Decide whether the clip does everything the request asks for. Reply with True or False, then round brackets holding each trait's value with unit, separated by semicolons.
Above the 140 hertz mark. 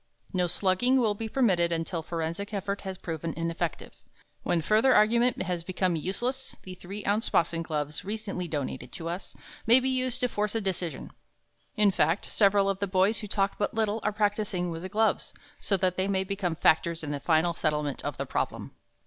True (190 Hz)